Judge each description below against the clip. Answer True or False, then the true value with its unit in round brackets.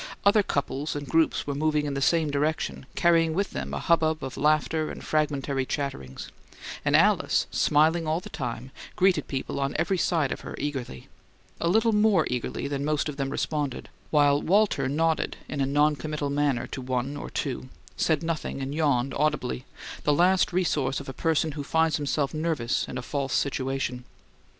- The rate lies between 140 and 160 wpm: False (180 wpm)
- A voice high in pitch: False (145 Hz)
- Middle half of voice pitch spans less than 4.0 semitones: True (2.8 semitones)